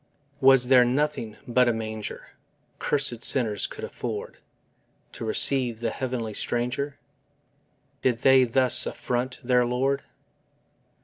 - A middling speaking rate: No, slow, 115 wpm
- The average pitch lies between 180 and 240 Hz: No, low, 125 Hz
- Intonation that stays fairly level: Yes, narrow, 2.1 semitones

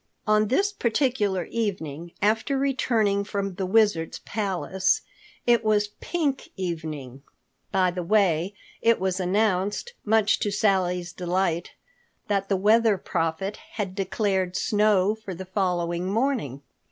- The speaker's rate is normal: No, slow, 120 wpm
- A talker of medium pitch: No, high, 195 Hz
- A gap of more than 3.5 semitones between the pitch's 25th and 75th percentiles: No, average, 3.2 semitones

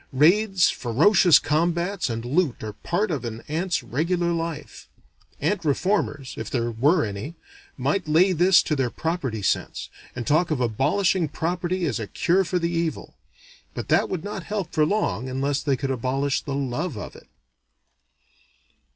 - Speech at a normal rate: Yes, average, 160 wpm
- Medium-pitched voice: Yes, medium, 155 Hz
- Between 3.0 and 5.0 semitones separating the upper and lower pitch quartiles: No, wide, 5.4 semitones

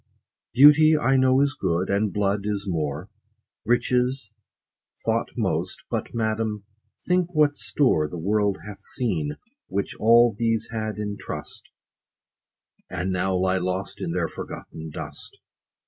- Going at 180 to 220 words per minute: No, slow, 135 wpm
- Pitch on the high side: No, low, 105 Hz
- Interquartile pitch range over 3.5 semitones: Yes, average, 4.8 semitones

